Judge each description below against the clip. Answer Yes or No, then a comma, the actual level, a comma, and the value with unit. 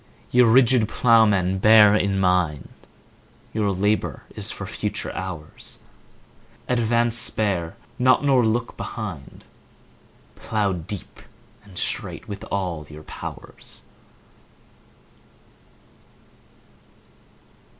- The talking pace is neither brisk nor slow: No, slow, 85 wpm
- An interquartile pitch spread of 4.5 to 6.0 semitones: No, average, 4.0 semitones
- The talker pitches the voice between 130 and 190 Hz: No, low, 105 Hz